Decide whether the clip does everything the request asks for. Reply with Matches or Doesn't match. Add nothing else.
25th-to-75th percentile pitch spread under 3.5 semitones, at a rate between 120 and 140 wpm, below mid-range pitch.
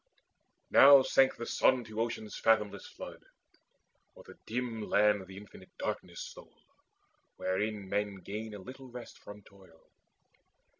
Matches